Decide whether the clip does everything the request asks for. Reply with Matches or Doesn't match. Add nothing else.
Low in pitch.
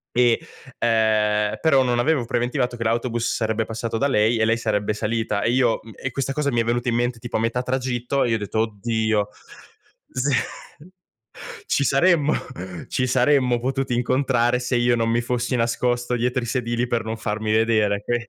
Matches